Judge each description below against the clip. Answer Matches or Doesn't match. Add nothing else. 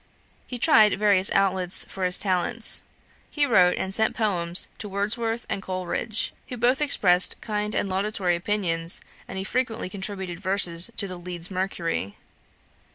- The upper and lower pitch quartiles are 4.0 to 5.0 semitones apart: Doesn't match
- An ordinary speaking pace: Matches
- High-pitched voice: Matches